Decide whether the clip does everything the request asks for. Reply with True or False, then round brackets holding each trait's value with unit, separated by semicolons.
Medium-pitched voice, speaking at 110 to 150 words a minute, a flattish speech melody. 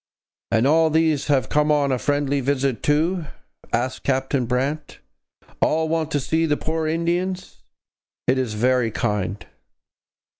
False (145 Hz; 140 wpm; 3.7 semitones)